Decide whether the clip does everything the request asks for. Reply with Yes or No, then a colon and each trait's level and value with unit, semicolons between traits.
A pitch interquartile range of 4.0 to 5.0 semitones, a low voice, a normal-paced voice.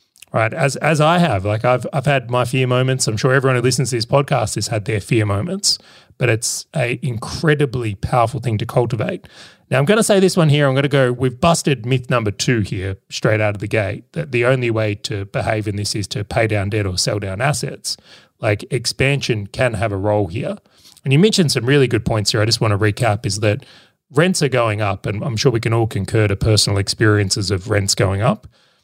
No: average, 4.5 semitones; low, 120 Hz; fast, 235 wpm